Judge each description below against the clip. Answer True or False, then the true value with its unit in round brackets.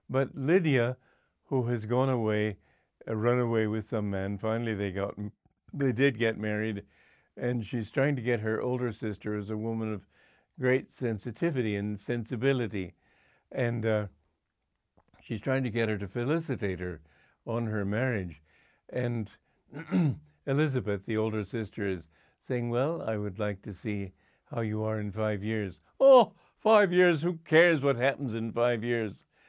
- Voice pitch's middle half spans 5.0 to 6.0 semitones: False (3.8 semitones)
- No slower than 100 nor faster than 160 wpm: True (155 wpm)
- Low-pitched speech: True (115 Hz)